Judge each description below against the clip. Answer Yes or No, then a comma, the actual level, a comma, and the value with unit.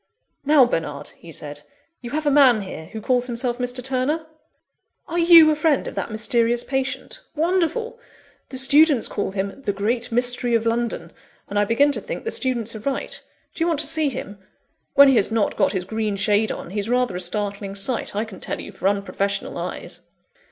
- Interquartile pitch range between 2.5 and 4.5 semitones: No, wide, 5.5 semitones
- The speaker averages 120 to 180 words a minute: No, average, 200 wpm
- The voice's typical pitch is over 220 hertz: Yes, high, 240 Hz